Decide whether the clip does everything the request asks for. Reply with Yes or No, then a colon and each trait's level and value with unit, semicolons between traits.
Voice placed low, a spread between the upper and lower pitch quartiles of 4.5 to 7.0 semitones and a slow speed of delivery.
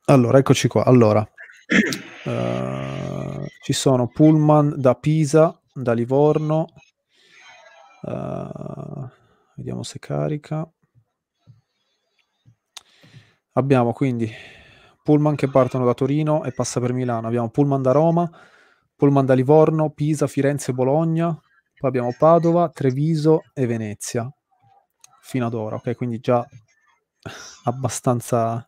No: low, 130 Hz; average, 4.0 semitones; slow, 105 wpm